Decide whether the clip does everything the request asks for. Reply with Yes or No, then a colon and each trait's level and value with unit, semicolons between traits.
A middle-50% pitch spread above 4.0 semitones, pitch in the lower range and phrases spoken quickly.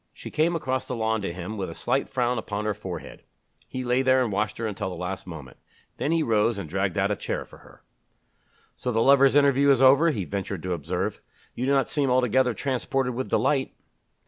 Yes: average, 4.9 semitones; low, 120 Hz; fast, 220 wpm